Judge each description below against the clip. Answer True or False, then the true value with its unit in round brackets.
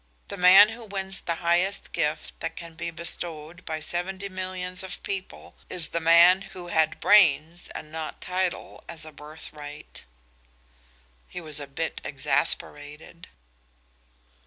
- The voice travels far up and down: False (3.0 semitones)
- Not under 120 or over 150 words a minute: True (135 wpm)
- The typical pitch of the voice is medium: True (170 Hz)